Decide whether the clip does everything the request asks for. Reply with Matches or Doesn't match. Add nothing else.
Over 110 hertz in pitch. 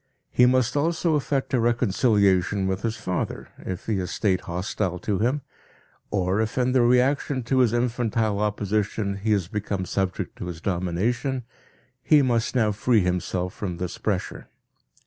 Doesn't match